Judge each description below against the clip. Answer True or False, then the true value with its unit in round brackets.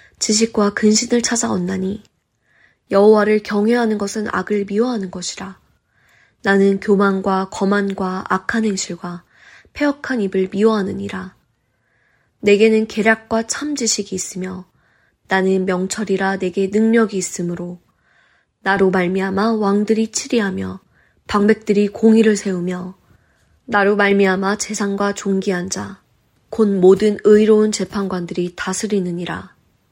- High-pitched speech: True (200 Hz)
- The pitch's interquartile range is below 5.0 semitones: True (2.4 semitones)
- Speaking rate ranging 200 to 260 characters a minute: False (270 characters per minute)